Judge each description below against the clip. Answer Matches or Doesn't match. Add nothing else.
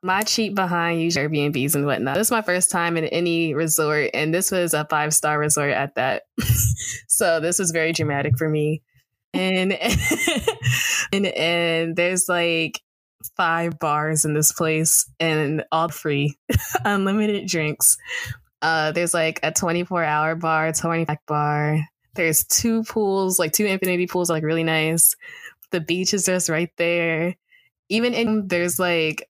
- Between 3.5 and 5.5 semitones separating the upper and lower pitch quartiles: Doesn't match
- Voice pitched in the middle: Matches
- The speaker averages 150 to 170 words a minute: Matches